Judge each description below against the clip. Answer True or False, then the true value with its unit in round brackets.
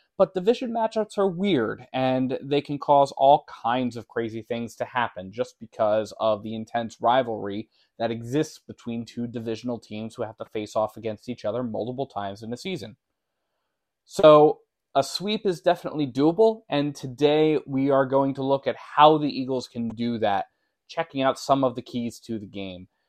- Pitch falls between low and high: False (130 Hz)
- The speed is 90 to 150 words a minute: False (180 wpm)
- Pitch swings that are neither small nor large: True (4.7 semitones)